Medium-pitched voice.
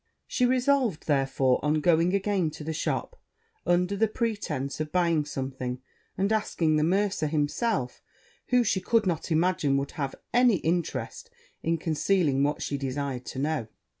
Yes: medium, 160 Hz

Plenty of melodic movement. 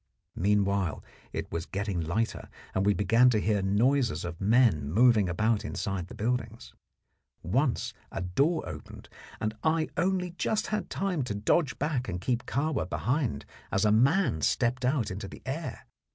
Yes: wide, 5.8 semitones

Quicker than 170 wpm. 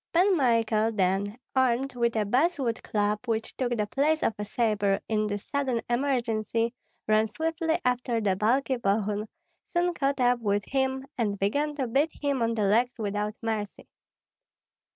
No: average, 160 wpm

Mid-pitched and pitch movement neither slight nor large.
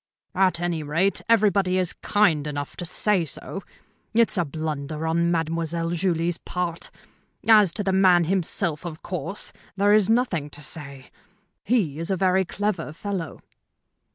Yes: medium, 175 Hz; average, 3.2 semitones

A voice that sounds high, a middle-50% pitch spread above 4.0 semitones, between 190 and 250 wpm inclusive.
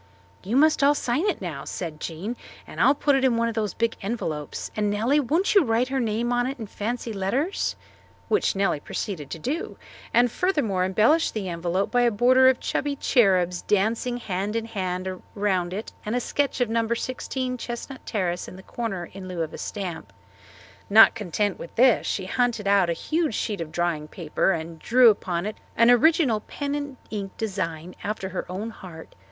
Yes: high, 215 Hz; average, 5.0 semitones; average, 195 wpm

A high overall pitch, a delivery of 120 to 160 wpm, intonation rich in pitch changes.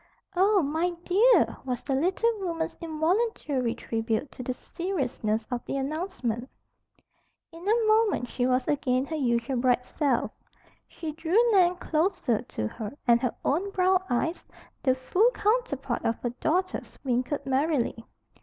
Yes: very high, 290 Hz; average, 145 wpm; wide, 6.6 semitones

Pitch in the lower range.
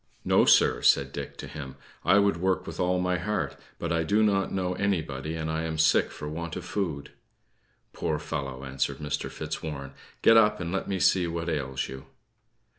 Yes: very low, 85 Hz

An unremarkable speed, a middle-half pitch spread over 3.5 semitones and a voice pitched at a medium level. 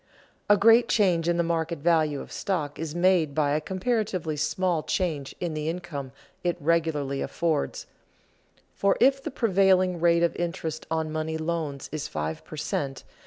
No: average, 165 wpm; average, 3.2 semitones; medium, 165 Hz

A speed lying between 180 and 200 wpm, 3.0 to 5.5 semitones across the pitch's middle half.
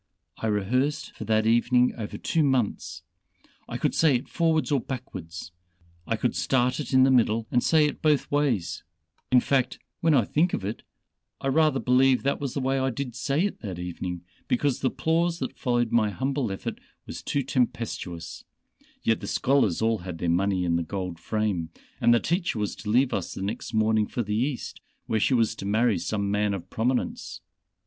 Yes: average, 195 wpm; average, 4.8 semitones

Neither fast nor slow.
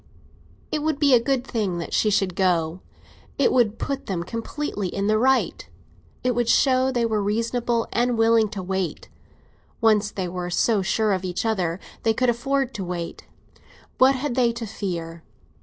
Yes: average, 175 wpm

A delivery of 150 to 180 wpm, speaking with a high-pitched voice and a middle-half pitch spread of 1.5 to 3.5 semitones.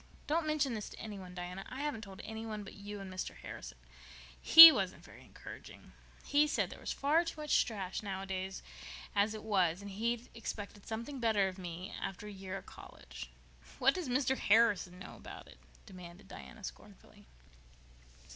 No: average, 175 wpm; high, 210 Hz; average, 4.0 semitones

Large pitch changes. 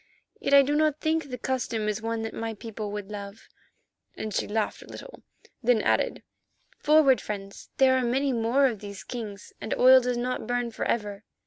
No: average, 3.7 semitones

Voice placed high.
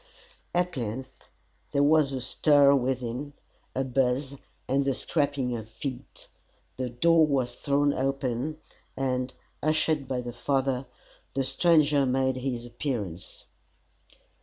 No: low, 135 Hz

